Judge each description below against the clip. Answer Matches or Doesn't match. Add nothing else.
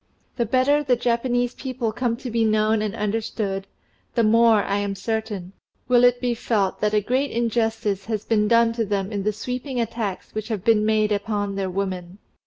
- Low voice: Doesn't match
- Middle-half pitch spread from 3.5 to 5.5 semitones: Doesn't match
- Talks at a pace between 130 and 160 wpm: Doesn't match